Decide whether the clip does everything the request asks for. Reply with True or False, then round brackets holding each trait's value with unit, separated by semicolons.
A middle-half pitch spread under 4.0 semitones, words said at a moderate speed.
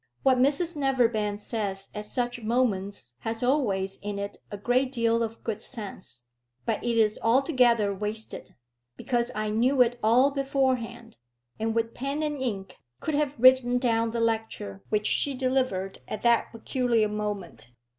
True (3.4 semitones; 155 wpm)